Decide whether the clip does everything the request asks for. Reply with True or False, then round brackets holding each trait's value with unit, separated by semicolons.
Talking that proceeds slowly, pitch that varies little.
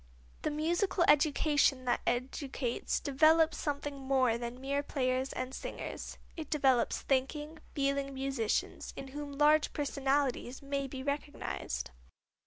True (120 wpm; 2.2 semitones)